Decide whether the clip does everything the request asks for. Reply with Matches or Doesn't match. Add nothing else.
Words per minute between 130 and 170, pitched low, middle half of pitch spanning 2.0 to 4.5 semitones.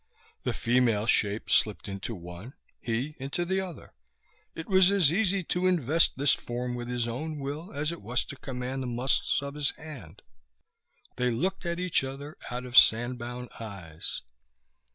Doesn't match